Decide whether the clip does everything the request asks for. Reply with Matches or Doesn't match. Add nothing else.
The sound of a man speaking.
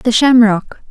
Doesn't match